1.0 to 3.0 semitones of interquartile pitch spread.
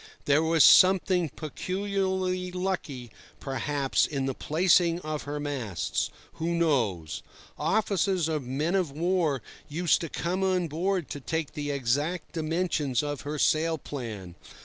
No: average, 4.2 semitones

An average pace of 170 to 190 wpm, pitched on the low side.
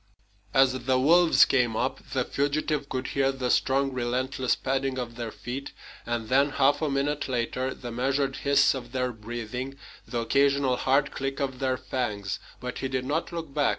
Yes: average, 180 wpm; low, 130 Hz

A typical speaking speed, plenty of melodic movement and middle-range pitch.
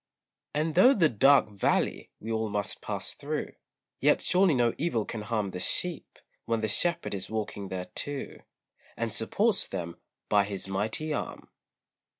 No: average, 155 wpm; wide, 7.1 semitones; low, 110 Hz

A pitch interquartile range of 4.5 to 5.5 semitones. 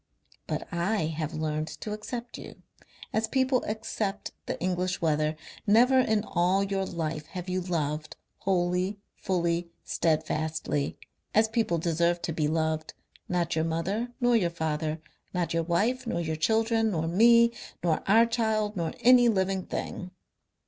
Yes: average, 5.2 semitones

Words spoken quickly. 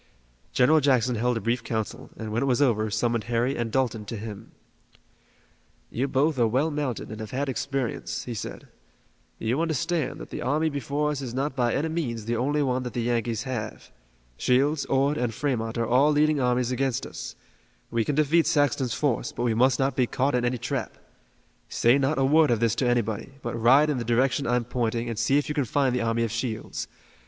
Yes: fast, 210 wpm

